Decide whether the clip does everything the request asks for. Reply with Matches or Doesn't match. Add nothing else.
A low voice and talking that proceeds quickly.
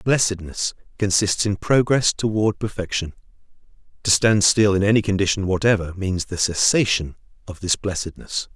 Doesn't match